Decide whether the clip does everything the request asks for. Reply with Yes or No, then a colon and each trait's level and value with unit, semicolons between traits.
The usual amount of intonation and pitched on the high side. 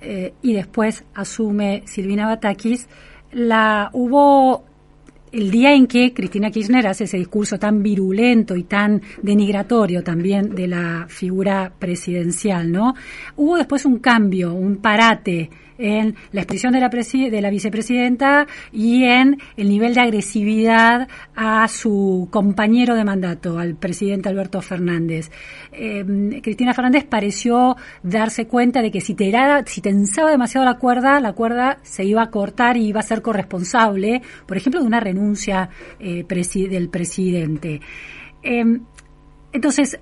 Yes: average, 4.1 semitones; high, 215 Hz